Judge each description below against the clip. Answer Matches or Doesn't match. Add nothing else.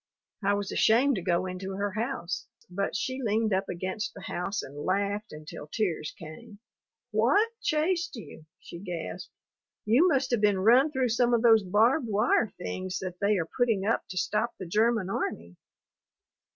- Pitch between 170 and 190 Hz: Doesn't match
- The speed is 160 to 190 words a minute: Matches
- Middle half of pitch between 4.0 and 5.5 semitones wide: Matches